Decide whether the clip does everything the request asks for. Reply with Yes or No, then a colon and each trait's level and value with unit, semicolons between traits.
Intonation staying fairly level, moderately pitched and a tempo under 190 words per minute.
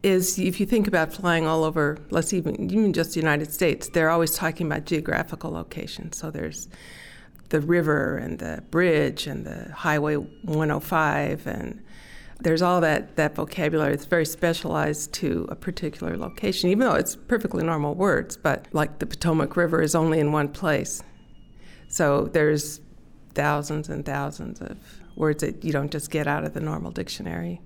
Yes: narrow, 2.3 semitones; medium, 155 Hz; average, 170 wpm